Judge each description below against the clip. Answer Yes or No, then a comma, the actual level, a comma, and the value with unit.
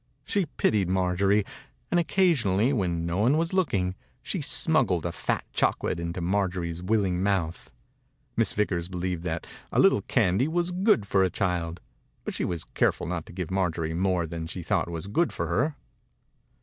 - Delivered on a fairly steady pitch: No, average, 3.7 semitones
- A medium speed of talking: Yes, average, 170 wpm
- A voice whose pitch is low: Yes, very low, 95 Hz